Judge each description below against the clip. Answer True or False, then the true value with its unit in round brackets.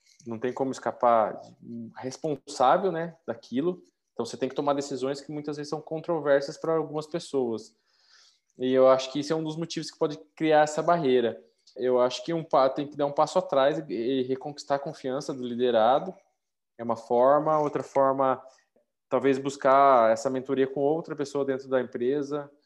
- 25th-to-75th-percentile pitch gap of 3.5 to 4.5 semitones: False (3.0 semitones)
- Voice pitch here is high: False (140 Hz)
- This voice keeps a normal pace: True (175 wpm)